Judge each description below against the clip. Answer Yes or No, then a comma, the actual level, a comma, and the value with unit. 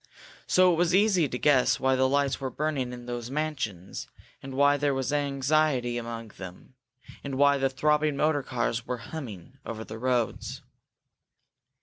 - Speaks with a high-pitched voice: No, low, 135 Hz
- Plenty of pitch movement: No, average, 3.3 semitones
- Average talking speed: Yes, average, 160 wpm